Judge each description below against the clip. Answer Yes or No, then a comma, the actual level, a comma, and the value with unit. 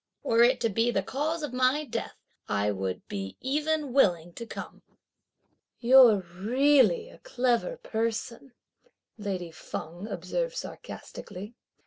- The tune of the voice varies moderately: No, wide, 6.6 semitones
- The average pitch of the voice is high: Yes, high, 235 Hz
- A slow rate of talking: Yes, slow, 125 wpm